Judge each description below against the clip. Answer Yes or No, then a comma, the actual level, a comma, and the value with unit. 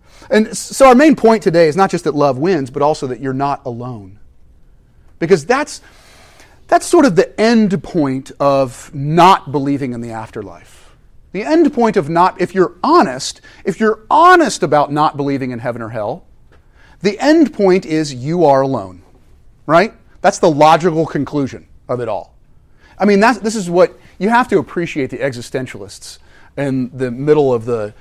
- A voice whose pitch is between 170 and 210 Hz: No, medium, 150 Hz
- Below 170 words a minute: No, average, 175 wpm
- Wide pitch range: Yes, wide, 7.3 semitones